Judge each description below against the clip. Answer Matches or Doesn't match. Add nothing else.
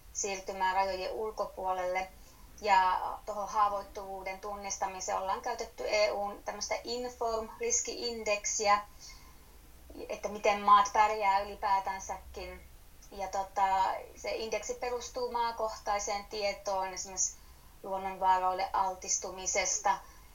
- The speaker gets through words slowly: Matches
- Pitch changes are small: Matches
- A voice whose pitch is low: Doesn't match